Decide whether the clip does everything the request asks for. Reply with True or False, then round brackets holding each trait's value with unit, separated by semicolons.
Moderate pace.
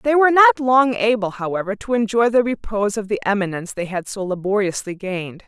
True (195 wpm)